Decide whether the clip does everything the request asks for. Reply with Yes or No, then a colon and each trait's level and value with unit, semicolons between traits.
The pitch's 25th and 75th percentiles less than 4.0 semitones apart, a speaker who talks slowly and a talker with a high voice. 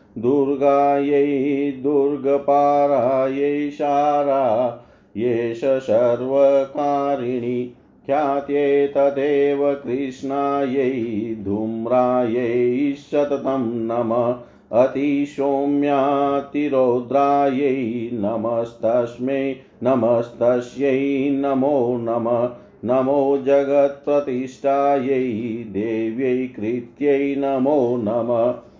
No: narrow, 2.5 semitones; slow, 45 wpm; low, 135 Hz